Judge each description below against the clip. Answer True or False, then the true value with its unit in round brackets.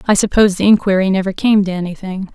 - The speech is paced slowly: False (205 wpm)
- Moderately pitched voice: False (195 Hz)